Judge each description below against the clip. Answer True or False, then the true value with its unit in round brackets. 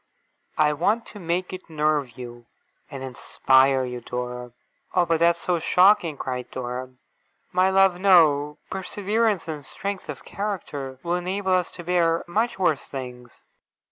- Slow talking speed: False (145 wpm)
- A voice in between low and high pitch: True (165 Hz)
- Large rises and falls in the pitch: True (5.9 semitones)